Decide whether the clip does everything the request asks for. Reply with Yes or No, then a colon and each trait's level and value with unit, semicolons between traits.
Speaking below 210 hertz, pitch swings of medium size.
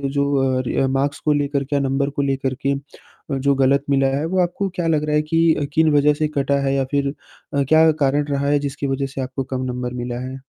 No: medium, 140 Hz; narrow, 1.6 semitones